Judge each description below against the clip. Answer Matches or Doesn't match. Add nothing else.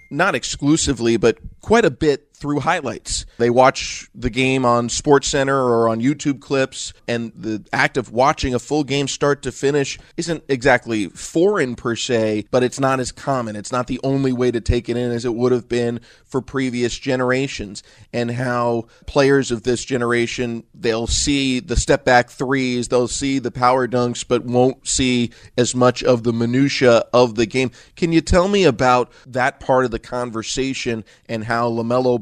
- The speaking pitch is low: Matches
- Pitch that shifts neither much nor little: Doesn't match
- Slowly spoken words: Doesn't match